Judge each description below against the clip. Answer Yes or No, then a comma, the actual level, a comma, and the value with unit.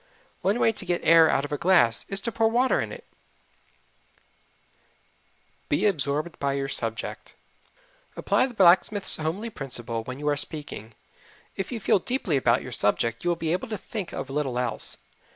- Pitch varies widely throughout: Yes, wide, 6.8 semitones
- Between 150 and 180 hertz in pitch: Yes, medium, 160 Hz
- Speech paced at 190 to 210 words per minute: No, average, 170 wpm